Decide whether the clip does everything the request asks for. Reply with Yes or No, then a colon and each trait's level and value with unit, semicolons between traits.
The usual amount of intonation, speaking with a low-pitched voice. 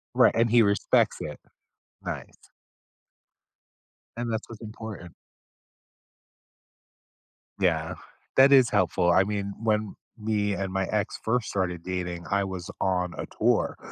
Yes: average, 3.2 semitones; low, 100 Hz